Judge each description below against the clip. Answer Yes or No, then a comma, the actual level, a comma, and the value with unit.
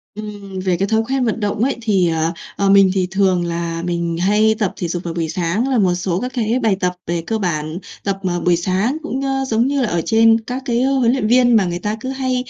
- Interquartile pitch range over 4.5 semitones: Yes, average, 5.1 semitones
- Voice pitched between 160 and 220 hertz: Yes, high, 200 Hz